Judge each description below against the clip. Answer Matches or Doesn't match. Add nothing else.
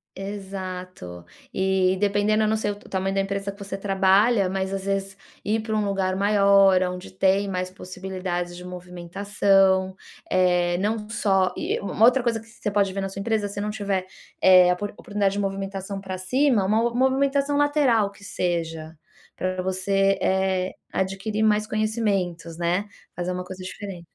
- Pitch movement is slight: Matches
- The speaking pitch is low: Doesn't match